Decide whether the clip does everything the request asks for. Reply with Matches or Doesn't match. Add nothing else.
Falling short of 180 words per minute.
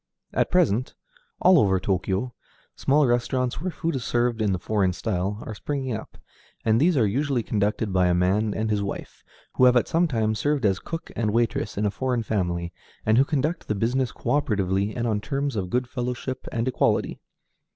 Doesn't match